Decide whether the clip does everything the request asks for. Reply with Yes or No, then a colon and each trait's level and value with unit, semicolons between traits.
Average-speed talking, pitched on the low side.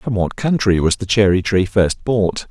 No: fast, 215 wpm; low, 100 Hz